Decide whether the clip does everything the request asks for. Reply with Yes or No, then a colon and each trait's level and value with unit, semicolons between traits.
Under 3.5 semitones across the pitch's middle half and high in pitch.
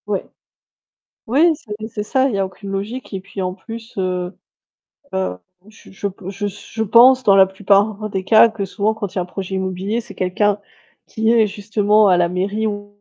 Yes: narrow, 2.4 semitones; high, 205 Hz